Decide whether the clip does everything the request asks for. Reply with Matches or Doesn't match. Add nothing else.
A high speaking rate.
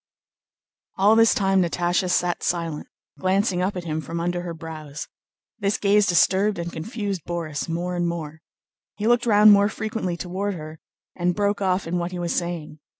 Doesn't match